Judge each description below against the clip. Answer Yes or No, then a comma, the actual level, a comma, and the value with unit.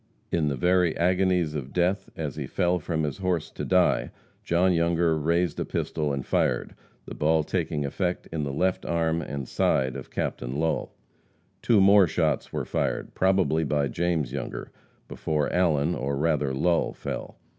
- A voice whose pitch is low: Yes, very low, 80 Hz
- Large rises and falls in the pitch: No, average, 3.3 semitones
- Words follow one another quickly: No, average, 165 wpm